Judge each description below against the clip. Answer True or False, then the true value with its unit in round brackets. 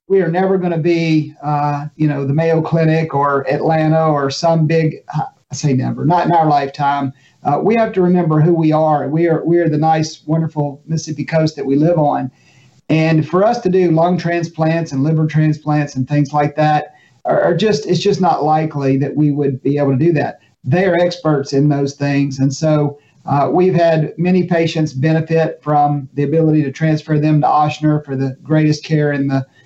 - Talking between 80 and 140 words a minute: False (205 wpm)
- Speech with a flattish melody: True (2.2 semitones)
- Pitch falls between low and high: True (155 Hz)